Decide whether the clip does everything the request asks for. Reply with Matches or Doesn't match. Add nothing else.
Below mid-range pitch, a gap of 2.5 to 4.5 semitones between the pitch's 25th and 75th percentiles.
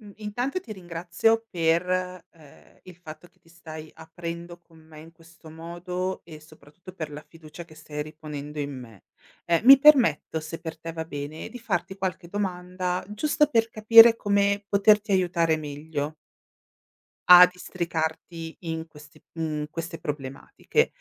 Doesn't match